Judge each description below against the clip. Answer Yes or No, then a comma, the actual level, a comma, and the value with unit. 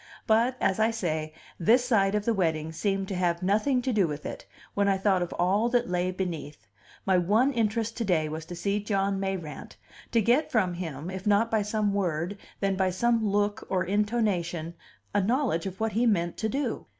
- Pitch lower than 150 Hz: No, high, 195 Hz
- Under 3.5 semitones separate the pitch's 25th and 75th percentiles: No, average, 3.8 semitones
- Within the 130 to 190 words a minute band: No, fast, 205 wpm